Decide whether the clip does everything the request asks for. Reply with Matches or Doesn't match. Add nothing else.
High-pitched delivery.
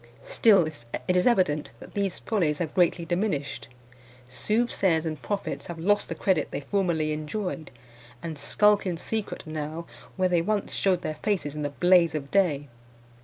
Doesn't match